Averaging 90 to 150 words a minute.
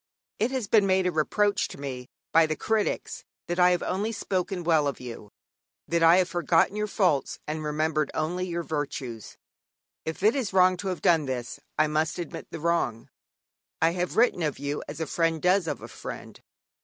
No: average, 195 wpm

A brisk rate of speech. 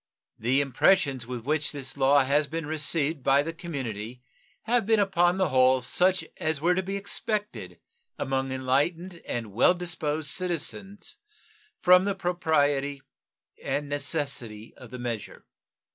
No: average, 140 wpm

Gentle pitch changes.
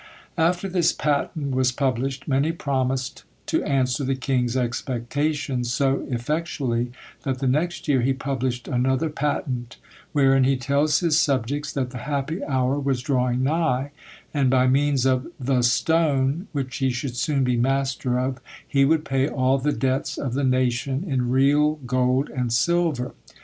Yes: narrow, 2.2 semitones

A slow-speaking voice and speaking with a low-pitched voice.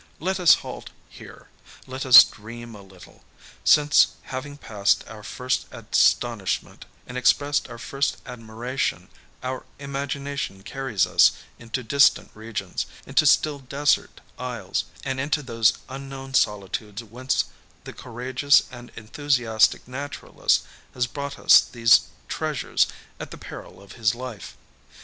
Yes: slow, 125 wpm; low, 125 Hz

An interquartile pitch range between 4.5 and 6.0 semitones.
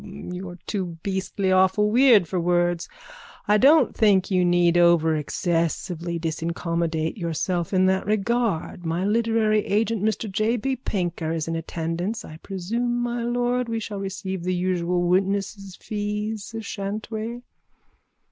No: average, 3.8 semitones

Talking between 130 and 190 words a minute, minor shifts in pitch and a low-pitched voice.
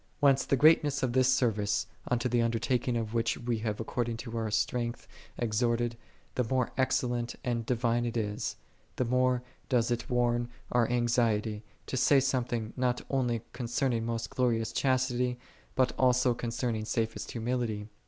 Yes: average, 160 wpm; narrow, 1.7 semitones; low, 120 Hz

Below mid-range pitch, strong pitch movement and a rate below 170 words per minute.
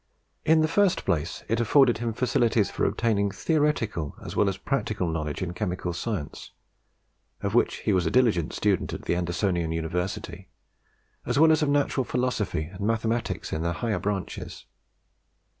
Yes: low, 105 Hz; wide, 5.9 semitones; average, 160 wpm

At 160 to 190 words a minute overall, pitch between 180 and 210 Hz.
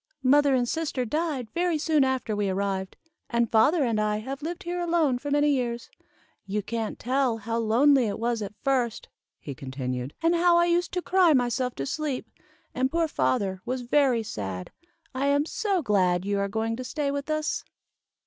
No: average, 185 wpm; very high, 255 Hz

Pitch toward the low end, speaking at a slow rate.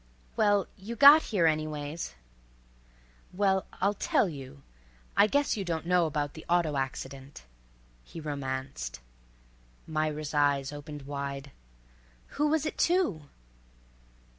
No: medium, 155 Hz; slow, 110 wpm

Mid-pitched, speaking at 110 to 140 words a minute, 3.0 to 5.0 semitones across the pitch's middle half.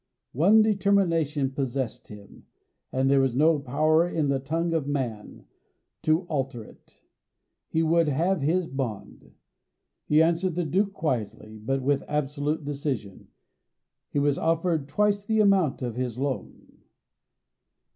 Yes: medium, 145 Hz; slow, 135 wpm; average, 3.9 semitones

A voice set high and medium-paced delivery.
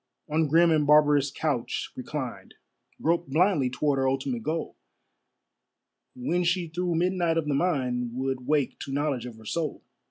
No: medium, 150 Hz; average, 155 wpm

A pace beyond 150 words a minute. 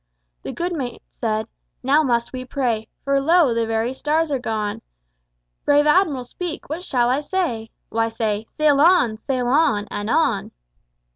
Yes: average, 160 wpm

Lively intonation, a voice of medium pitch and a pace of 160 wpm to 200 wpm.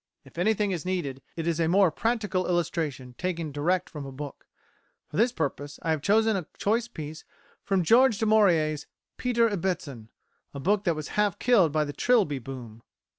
Yes: wide, 5.8 semitones; medium, 175 Hz; average, 180 wpm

